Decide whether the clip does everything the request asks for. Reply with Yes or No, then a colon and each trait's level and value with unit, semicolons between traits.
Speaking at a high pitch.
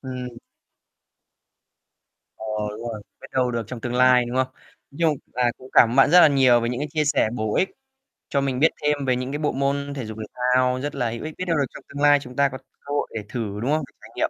No: low, 130 Hz